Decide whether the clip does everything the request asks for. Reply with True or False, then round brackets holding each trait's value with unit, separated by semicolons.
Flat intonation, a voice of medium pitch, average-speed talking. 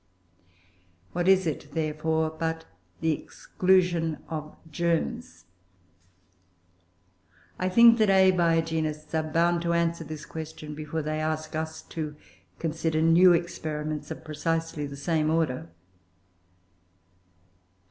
False (1.6 semitones; 160 Hz; 105 wpm)